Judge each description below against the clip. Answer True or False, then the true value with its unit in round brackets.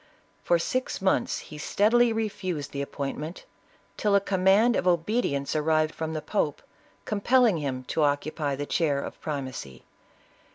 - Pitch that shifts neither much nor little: False (6.2 semitones)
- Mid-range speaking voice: True (160 Hz)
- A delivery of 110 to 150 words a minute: True (140 wpm)